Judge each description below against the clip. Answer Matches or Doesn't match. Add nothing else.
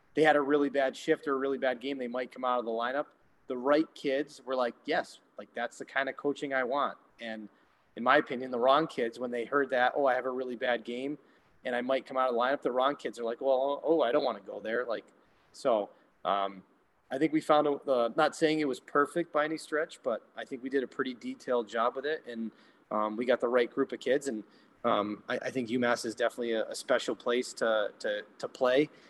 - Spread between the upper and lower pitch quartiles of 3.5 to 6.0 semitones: Doesn't match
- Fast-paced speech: Matches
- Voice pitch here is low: Matches